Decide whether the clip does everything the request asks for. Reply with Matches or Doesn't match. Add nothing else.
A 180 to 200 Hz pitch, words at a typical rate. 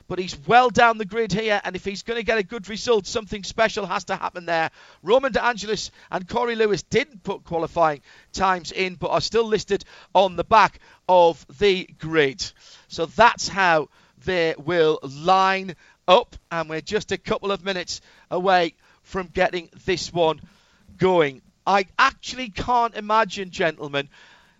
Matches